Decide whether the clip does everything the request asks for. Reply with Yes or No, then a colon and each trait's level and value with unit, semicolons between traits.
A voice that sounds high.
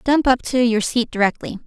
Yes: high, 240 Hz